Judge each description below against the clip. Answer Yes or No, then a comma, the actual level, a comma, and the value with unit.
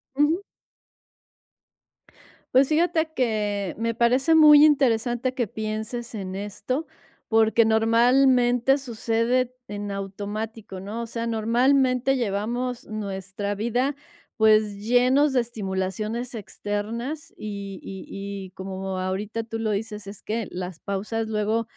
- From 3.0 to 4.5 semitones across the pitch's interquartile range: Yes, average, 3.4 semitones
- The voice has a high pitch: Yes, high, 225 Hz